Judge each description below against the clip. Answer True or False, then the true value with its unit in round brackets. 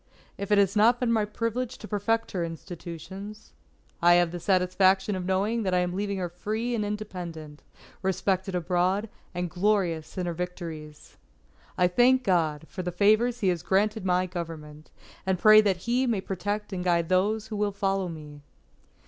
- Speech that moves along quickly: False (175 wpm)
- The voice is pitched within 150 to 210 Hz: True (190 Hz)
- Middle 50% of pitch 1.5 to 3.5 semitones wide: True (3.0 semitones)